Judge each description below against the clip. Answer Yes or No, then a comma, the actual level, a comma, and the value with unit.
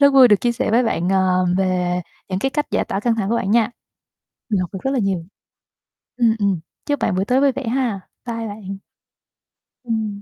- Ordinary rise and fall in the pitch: Yes, average, 4.3 semitones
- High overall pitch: Yes, high, 220 Hz